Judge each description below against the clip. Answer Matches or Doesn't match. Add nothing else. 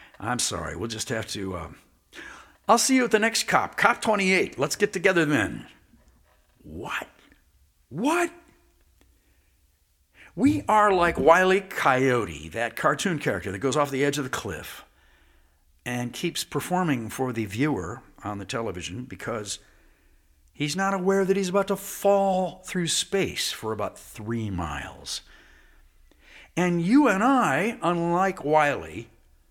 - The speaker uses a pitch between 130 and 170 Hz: Matches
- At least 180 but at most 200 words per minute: Doesn't match